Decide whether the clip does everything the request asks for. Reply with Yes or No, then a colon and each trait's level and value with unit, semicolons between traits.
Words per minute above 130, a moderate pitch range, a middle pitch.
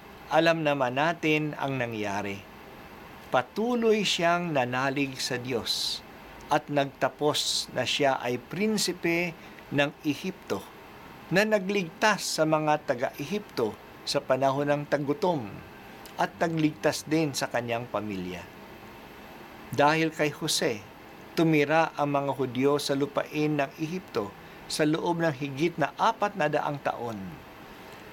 No: average, 115 wpm; average, 3.6 semitones; medium, 150 Hz